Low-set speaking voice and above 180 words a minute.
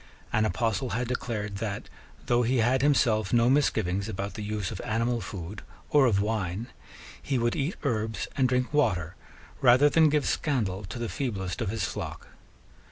No: low, 115 Hz; average, 170 wpm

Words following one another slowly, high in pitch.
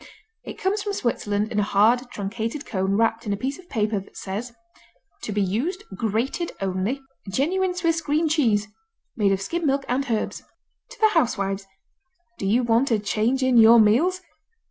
No: average, 175 wpm; high, 230 Hz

